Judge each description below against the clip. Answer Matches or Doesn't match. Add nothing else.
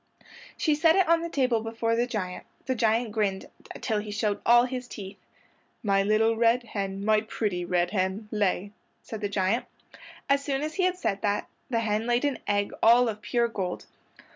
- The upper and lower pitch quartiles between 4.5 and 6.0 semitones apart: Doesn't match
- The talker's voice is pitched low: Doesn't match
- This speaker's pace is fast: Doesn't match